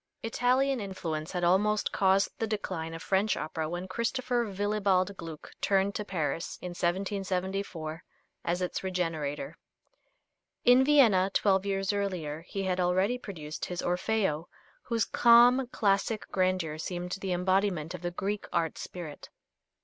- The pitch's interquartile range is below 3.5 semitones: Yes, average, 2.9 semitones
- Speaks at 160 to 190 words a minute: No, slow, 135 wpm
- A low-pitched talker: No, high, 190 Hz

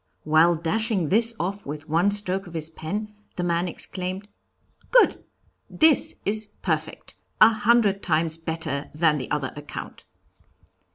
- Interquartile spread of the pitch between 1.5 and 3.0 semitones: No, average, 4.6 semitones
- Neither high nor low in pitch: Yes, medium, 175 Hz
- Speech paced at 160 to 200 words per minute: No, slow, 135 wpm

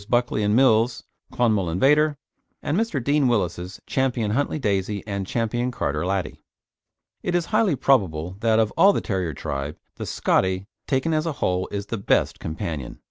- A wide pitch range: Yes, wide, 6.7 semitones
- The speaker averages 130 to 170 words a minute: Yes, average, 165 wpm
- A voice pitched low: Yes, low, 110 Hz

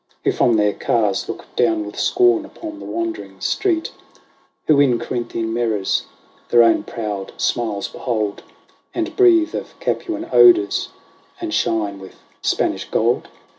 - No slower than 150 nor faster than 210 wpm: No, slow, 135 wpm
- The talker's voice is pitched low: Yes, low, 120 Hz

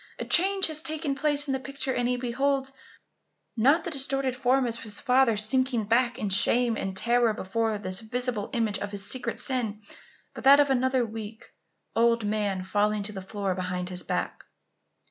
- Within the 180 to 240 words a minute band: Yes, average, 185 wpm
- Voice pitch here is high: Yes, high, 235 Hz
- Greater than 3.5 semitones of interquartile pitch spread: Yes, average, 4.2 semitones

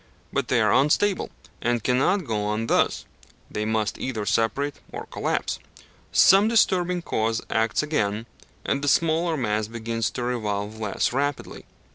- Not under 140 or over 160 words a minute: Yes, average, 145 wpm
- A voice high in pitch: No, low, 120 Hz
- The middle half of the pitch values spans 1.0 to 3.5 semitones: No, wide, 5.5 semitones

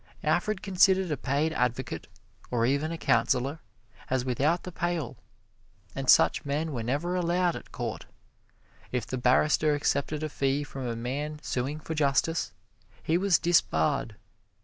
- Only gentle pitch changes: No, average, 4.2 semitones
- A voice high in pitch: No, medium, 145 Hz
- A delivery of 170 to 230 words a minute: No, average, 150 wpm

